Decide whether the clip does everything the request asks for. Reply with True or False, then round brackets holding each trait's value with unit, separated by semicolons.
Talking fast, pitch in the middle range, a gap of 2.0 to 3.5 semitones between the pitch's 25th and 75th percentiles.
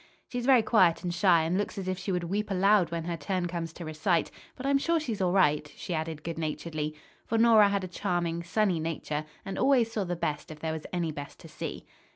False (235 wpm; 175 Hz; 3.9 semitones)